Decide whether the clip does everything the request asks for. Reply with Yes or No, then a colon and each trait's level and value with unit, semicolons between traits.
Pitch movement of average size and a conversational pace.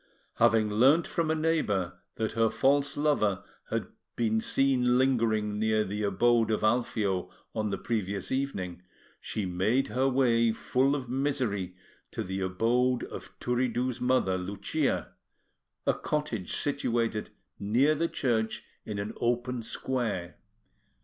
No: average, 3.8 semitones; slow, 130 wpm